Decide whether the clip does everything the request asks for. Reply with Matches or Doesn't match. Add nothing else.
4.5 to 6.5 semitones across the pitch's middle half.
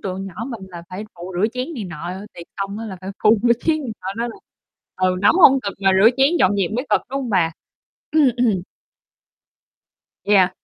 Matches